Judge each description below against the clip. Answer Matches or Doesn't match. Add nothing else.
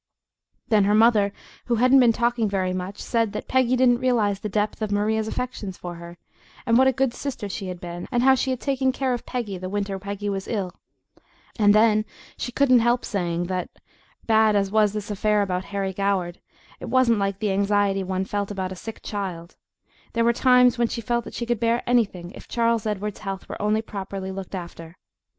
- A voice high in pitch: Matches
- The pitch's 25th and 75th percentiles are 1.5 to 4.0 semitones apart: Matches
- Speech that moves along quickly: Matches